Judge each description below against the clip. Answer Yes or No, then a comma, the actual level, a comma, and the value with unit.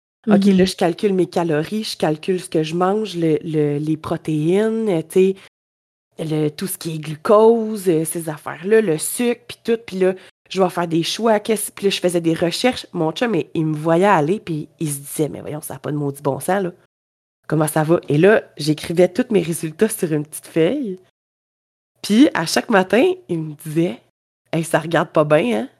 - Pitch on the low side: No, medium, 170 Hz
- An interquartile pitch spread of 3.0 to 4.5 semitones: Yes, average, 3.8 semitones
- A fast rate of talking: No, average, 205 wpm